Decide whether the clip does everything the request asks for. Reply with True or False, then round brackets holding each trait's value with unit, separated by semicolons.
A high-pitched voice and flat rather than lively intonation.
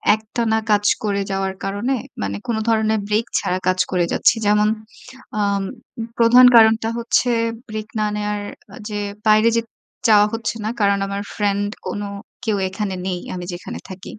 True (210 Hz; 1.8 semitones)